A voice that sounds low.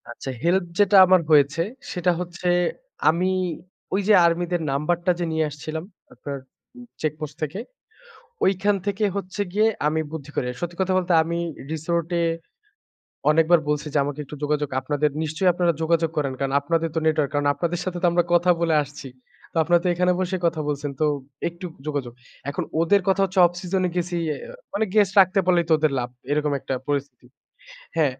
No: medium, 165 Hz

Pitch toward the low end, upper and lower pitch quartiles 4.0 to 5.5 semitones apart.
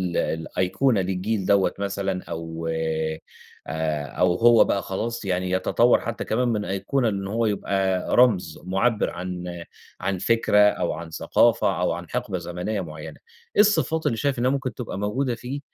Yes: low, 100 Hz; average, 4.5 semitones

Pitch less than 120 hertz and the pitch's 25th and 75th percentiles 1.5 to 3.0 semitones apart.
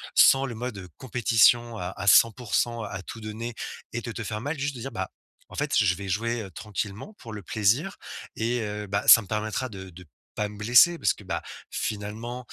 Yes: low, 110 Hz; average, 2.7 semitones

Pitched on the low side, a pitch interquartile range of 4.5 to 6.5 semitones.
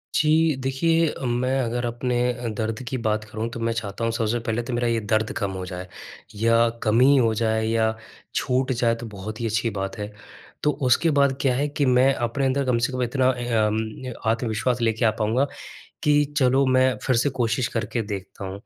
No: low, 115 Hz; average, 2.7 semitones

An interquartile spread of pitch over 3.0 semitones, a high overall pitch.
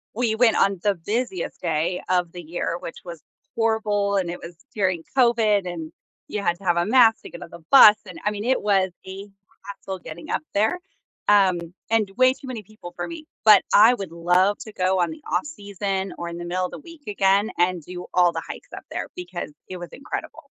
Yes: average, 3.7 semitones; high, 195 Hz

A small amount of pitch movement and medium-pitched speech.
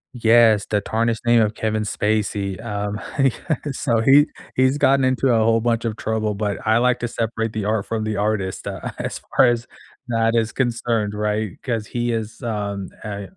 No: narrow, 2.0 semitones; low, 110 Hz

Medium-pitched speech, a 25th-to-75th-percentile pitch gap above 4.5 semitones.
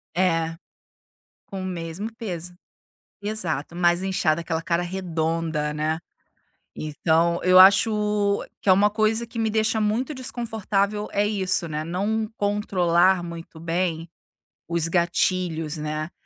No: medium, 180 Hz; average, 4.0 semitones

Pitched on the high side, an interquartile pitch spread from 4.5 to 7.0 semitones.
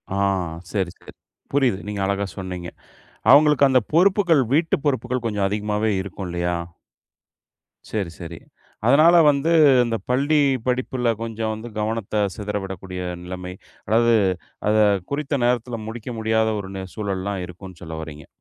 No: low, 110 Hz; average, 5.0 semitones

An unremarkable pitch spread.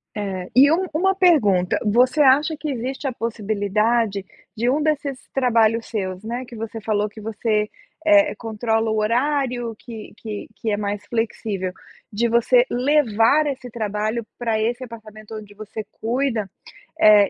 Yes: average, 3.3 semitones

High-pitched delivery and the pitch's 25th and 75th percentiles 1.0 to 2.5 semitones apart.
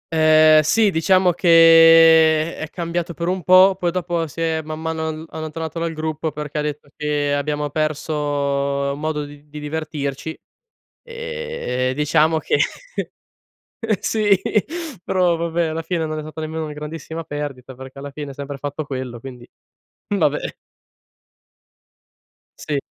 No: medium, 155 Hz; narrow, 2.1 semitones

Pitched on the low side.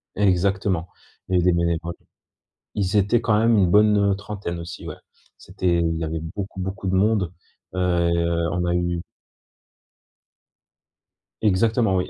Yes: very low, 95 Hz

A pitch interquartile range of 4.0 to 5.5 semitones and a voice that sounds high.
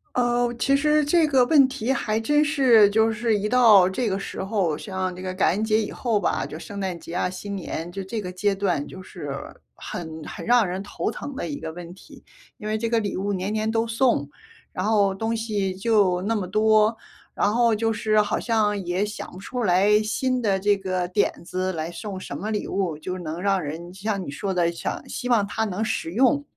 No: average, 3.5 semitones; high, 205 Hz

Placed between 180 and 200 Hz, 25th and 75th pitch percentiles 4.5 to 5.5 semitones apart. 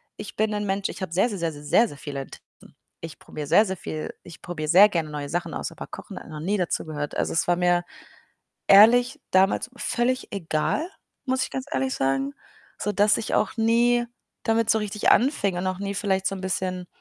Yes: high, 190 Hz; average, 4.8 semitones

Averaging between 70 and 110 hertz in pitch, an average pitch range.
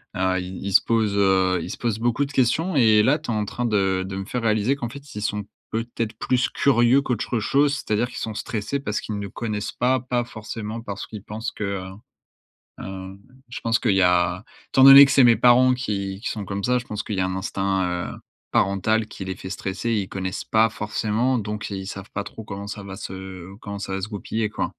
Yes: low, 105 Hz; average, 3.6 semitones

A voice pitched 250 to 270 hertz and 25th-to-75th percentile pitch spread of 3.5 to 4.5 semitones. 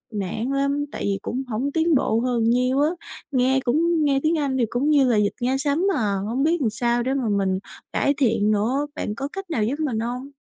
Yes: very high, 260 Hz; average, 3.9 semitones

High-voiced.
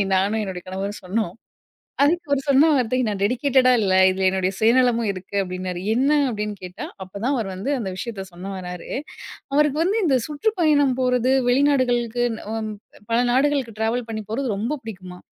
Yes: high, 230 Hz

